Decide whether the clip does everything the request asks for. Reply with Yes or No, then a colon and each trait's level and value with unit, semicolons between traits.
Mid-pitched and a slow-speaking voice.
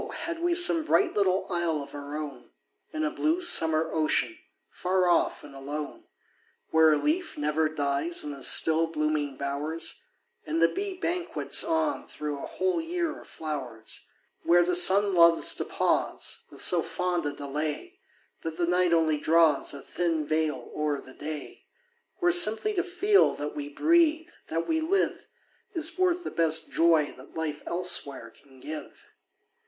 No: medium, 165 Hz; average, 165 wpm